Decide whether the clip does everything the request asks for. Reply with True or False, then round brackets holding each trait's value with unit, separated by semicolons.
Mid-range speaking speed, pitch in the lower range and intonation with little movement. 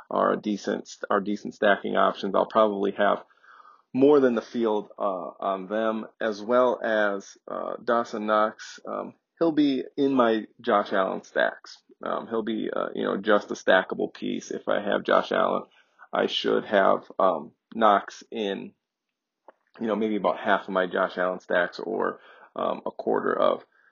True (170 wpm; 110 Hz; 2.3 semitones)